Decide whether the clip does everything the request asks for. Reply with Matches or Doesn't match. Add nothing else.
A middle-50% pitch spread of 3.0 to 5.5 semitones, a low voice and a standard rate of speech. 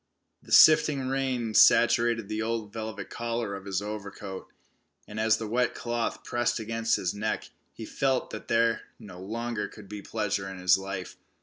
Doesn't match